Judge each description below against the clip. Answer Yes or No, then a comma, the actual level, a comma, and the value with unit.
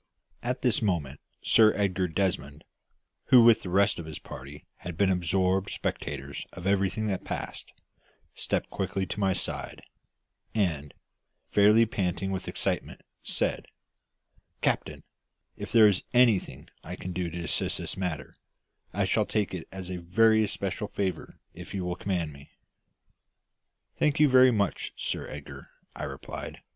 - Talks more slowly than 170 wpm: Yes, average, 150 wpm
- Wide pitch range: No, average, 3.3 semitones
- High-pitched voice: No, very low, 95 Hz